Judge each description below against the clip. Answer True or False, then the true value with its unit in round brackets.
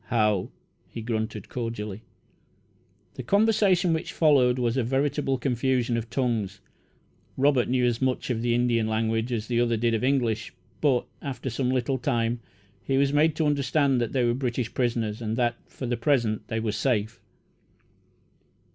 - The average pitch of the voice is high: False (120 Hz)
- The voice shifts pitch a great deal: False (2.9 semitones)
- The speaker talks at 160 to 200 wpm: True (165 wpm)